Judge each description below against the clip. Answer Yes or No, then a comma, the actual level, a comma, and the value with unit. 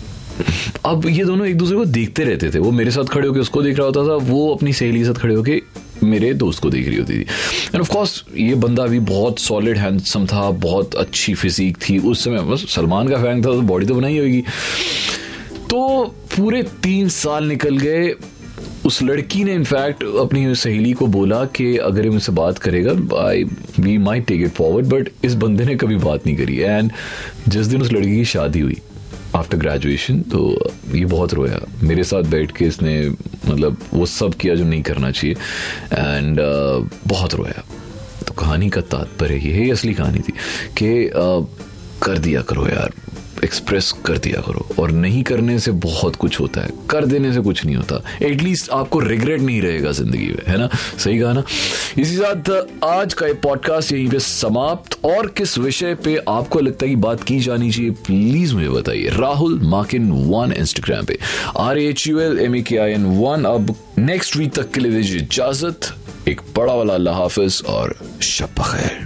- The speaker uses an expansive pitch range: Yes, wide, 6.7 semitones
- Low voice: Yes, low, 115 Hz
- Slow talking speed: No, fast, 190 wpm